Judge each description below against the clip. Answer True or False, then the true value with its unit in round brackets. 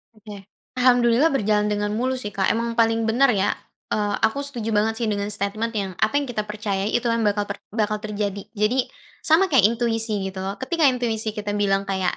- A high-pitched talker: True (215 Hz)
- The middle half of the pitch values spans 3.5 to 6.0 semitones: False (2.6 semitones)